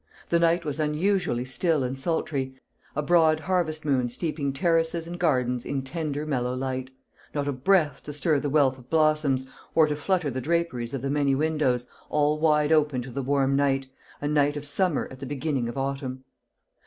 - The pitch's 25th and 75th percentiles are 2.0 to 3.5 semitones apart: Yes, average, 3.0 semitones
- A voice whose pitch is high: No, medium, 145 Hz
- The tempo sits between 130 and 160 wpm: No, average, 190 wpm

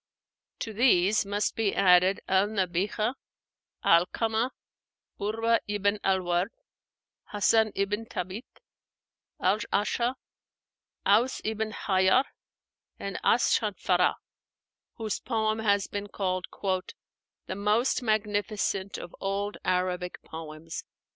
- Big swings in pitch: No, average, 2.7 semitones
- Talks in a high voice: Yes, high, 205 Hz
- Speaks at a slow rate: Yes, slow, 100 wpm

